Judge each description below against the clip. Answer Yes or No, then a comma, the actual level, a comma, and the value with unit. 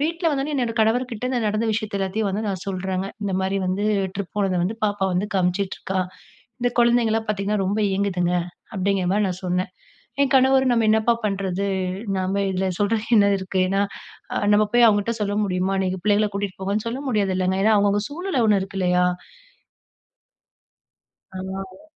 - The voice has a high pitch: Yes, high, 200 Hz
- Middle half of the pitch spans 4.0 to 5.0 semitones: No, narrow, 2.6 semitones